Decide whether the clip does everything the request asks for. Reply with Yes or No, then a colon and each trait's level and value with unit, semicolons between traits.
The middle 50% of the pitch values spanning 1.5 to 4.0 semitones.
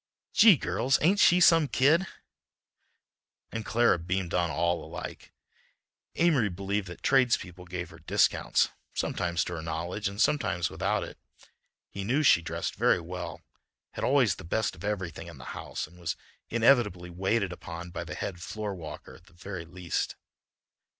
No: wide, 5.4 semitones